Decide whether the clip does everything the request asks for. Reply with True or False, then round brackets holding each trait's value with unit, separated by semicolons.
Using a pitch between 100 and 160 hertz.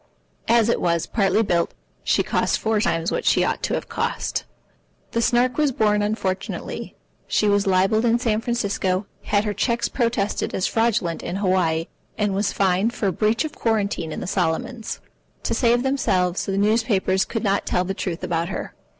False (205 Hz)